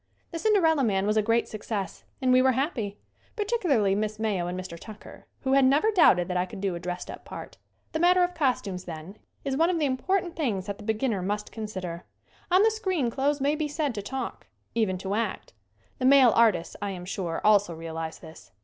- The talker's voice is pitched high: Yes, high, 220 Hz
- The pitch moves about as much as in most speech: No, wide, 7.2 semitones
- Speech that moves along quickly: Yes, fast, 215 wpm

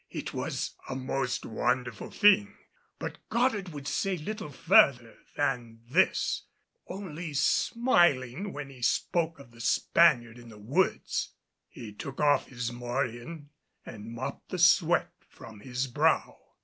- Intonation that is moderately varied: No, wide, 6.0 semitones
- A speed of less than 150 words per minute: Yes, slow, 135 wpm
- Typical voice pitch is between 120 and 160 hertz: Yes, low, 135 Hz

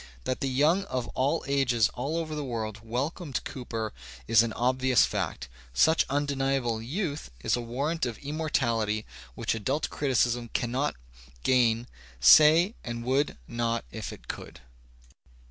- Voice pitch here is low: Yes, low, 130 Hz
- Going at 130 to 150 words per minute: Yes, average, 145 wpm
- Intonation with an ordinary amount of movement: Yes, average, 3.7 semitones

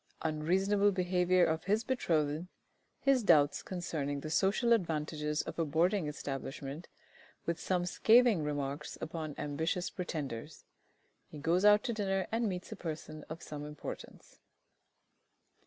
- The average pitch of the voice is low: No, medium, 165 Hz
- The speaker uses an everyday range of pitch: Yes, average, 4.3 semitones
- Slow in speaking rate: Yes, slow, 130 wpm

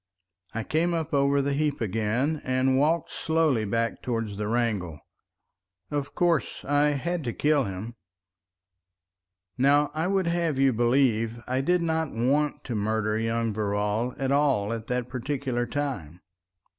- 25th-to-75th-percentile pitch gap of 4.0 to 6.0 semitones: Yes, average, 4.5 semitones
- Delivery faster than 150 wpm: No, average, 145 wpm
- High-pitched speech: No, low, 130 Hz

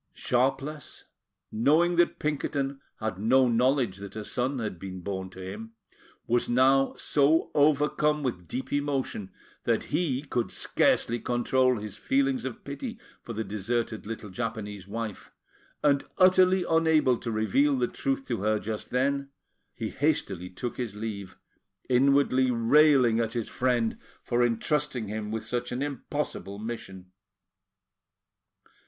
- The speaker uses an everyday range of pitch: Yes, average, 4.7 semitones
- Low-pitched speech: Yes, low, 125 Hz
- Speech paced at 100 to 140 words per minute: Yes, slow, 135 wpm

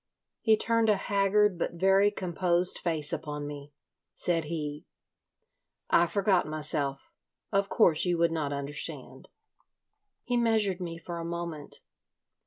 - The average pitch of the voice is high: No, medium, 170 Hz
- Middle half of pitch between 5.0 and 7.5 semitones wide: No, average, 4.4 semitones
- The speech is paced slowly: Yes, slow, 130 wpm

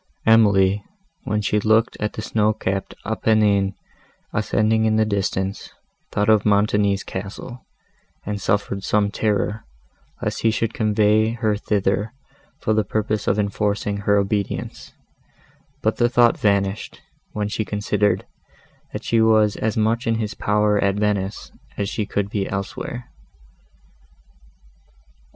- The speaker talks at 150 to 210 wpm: No, slow, 135 wpm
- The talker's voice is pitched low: Yes, low, 105 Hz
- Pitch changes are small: Yes, narrow, 1.4 semitones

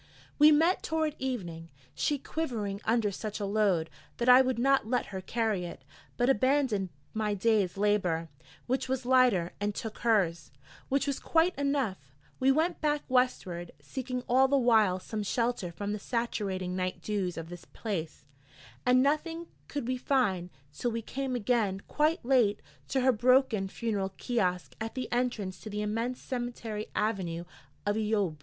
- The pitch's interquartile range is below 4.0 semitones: No, average, 4.8 semitones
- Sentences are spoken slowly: No, average, 165 wpm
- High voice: Yes, high, 225 Hz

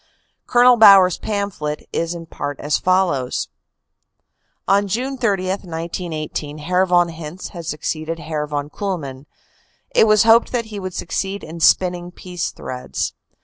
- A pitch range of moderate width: Yes, average, 4.2 semitones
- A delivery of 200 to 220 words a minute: No, average, 145 wpm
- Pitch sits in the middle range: Yes, medium, 175 Hz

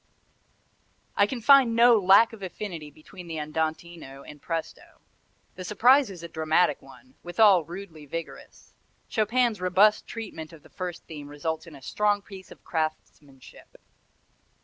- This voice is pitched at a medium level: Yes, medium, 180 Hz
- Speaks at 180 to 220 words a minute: No, average, 145 wpm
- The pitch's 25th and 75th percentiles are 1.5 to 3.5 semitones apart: No, average, 4.9 semitones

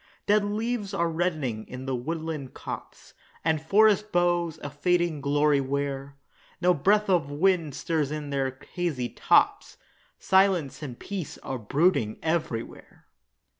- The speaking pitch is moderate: Yes, medium, 160 Hz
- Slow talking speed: Yes, slow, 130 wpm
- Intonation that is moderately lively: Yes, average, 4.5 semitones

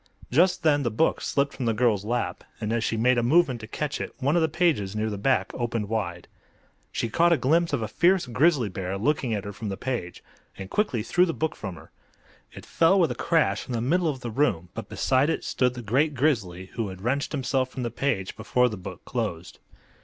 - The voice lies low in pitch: Yes, low, 125 Hz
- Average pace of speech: No, fast, 235 wpm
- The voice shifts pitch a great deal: Yes, wide, 5.7 semitones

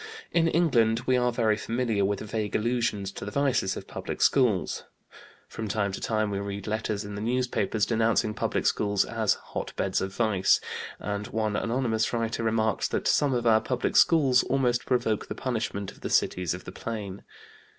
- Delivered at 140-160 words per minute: No, average, 180 wpm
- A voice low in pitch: Yes, low, 110 Hz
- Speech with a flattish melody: No, average, 3.0 semitones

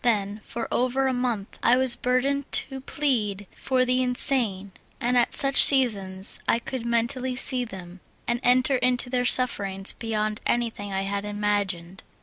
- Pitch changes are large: No, average, 3.8 semitones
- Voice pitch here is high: Yes, high, 240 Hz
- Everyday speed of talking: Yes, average, 160 wpm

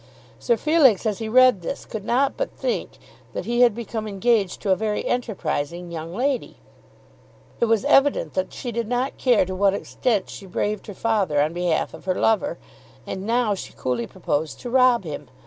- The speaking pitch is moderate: No, high, 215 Hz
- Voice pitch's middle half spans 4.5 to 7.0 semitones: Yes, average, 4.9 semitones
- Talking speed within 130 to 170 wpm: No, average, 190 wpm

